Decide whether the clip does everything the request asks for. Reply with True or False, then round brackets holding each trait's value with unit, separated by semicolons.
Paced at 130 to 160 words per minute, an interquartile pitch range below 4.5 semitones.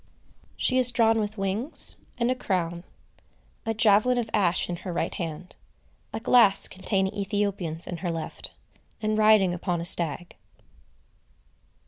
True (140 wpm; 3.9 semitones)